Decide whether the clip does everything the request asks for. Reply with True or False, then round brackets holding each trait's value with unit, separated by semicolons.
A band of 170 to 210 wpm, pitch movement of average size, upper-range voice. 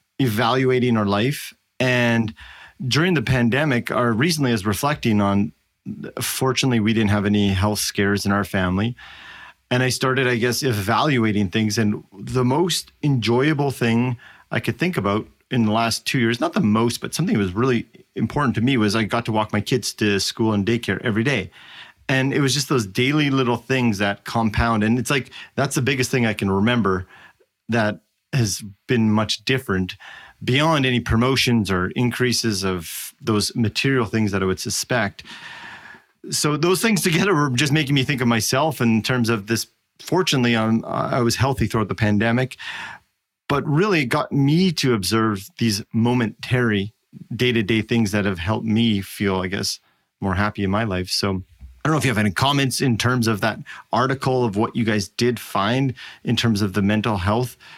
False (185 wpm; 3.6 semitones; 115 Hz)